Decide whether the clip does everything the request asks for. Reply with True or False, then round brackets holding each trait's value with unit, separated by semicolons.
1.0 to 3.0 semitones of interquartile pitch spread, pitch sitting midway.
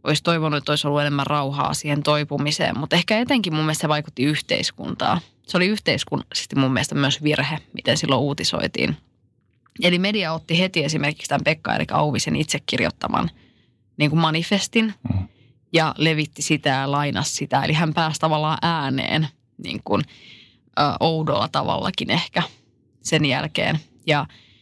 True (2.6 semitones; 150 Hz)